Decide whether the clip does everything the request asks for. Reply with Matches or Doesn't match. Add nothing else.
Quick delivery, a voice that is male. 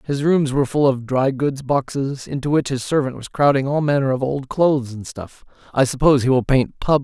Matches